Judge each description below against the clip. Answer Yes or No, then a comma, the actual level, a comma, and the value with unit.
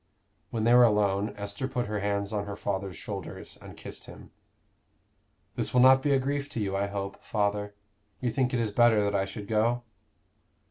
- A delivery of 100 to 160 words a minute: No, average, 195 wpm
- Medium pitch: No, low, 105 Hz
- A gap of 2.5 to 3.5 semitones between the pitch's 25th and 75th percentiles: Yes, average, 3.2 semitones